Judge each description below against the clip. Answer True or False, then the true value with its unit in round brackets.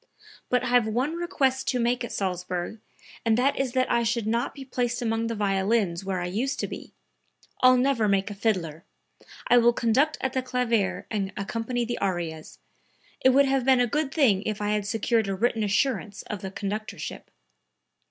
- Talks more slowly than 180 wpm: False (190 wpm)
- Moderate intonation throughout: True (4.1 semitones)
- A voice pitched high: True (230 Hz)